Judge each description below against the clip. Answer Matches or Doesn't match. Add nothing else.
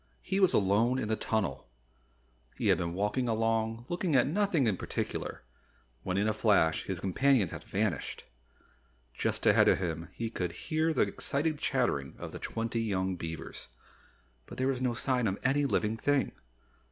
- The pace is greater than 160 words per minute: Matches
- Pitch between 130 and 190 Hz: Doesn't match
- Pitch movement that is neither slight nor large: Doesn't match